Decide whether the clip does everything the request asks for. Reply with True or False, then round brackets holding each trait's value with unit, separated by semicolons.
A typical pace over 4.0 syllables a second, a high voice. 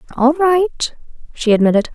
True (4.9 syllables/s; 280 Hz)